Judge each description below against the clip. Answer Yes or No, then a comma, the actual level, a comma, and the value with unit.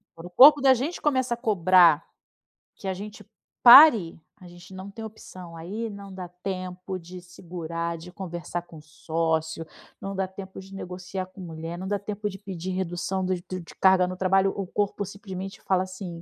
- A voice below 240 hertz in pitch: Yes, medium, 185 Hz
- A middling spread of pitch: No, narrow, 2.2 semitones